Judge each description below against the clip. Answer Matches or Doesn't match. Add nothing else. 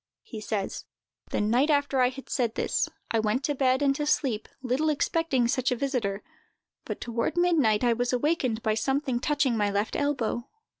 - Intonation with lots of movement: Doesn't match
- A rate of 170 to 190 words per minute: Matches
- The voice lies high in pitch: Matches